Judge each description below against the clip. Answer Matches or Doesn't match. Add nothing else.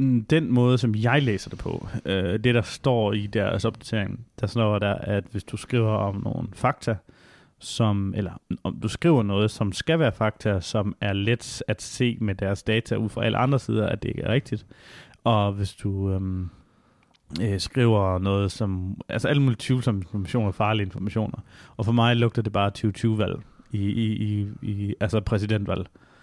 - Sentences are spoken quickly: Doesn't match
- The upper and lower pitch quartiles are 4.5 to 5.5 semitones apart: Doesn't match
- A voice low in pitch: Matches